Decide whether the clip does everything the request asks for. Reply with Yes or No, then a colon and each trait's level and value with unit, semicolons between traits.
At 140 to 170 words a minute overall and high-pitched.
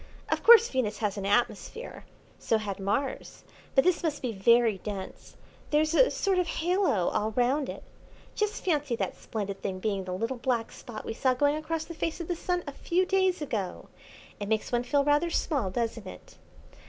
No: average, 190 wpm; very high, 255 Hz